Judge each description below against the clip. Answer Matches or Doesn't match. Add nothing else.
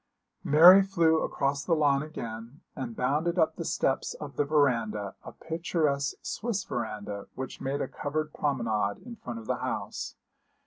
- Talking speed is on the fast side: Doesn't match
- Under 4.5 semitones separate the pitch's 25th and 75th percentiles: Doesn't match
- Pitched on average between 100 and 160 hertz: Matches